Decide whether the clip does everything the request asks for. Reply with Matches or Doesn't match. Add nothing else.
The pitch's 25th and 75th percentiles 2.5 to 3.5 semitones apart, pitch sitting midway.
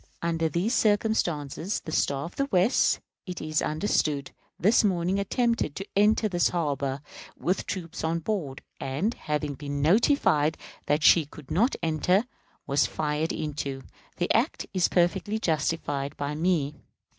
Doesn't match